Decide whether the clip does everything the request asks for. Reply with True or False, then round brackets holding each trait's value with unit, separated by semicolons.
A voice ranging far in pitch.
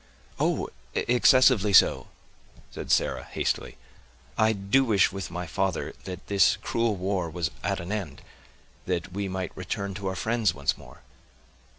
False (2.9 semitones)